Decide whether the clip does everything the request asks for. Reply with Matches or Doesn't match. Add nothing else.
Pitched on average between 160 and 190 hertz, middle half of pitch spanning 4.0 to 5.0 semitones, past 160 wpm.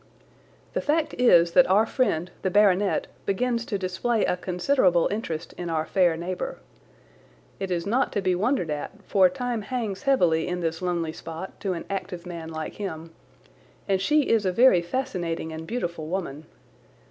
Matches